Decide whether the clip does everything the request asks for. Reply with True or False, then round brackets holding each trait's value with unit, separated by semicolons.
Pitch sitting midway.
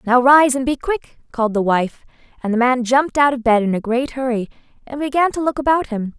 False (255 Hz)